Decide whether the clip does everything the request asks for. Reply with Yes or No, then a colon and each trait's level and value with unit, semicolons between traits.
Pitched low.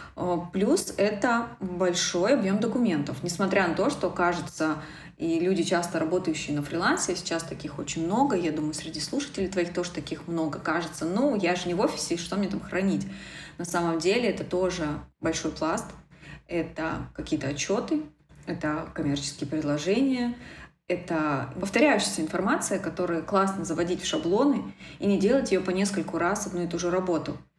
No: medium, 175 Hz